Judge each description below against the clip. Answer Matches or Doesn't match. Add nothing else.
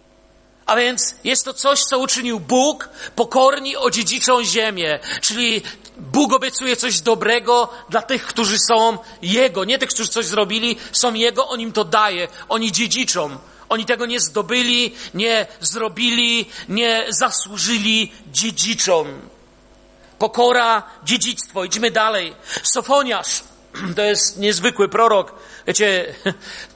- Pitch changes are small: Matches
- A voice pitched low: Doesn't match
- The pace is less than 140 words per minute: Matches